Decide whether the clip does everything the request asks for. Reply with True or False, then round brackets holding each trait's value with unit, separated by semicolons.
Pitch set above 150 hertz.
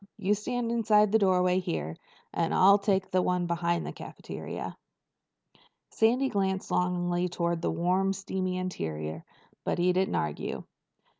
True (185 Hz)